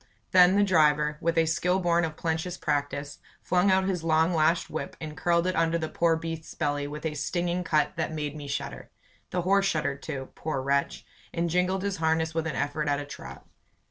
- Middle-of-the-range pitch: Yes, medium, 160 Hz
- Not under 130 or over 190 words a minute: No, fast, 205 wpm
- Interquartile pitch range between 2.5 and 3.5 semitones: Yes, average, 2.8 semitones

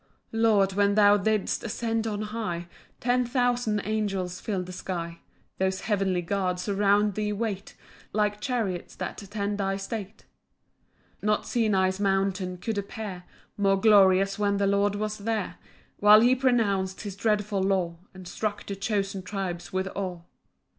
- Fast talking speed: No, average, 150 wpm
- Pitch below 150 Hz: No, high, 200 Hz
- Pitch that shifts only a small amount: Yes, narrow, 2.0 semitones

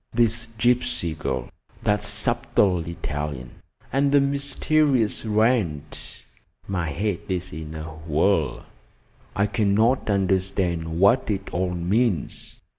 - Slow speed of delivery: Yes, slow, 110 wpm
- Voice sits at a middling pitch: No, low, 100 Hz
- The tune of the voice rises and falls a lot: Yes, wide, 5.9 semitones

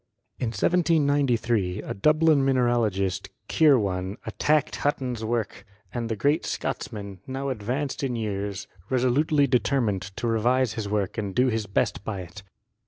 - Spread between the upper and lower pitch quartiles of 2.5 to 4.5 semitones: No, average, 4.9 semitones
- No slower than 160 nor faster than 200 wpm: No, average, 140 wpm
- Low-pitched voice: Yes, low, 120 Hz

